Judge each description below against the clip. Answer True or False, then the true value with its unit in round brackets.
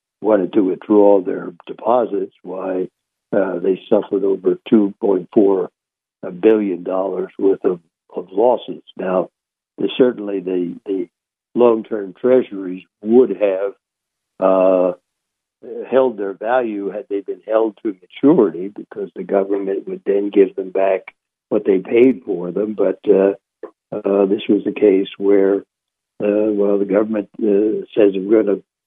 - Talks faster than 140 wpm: False (135 wpm)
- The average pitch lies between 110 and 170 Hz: False (100 Hz)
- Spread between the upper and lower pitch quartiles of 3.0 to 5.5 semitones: False (2.5 semitones)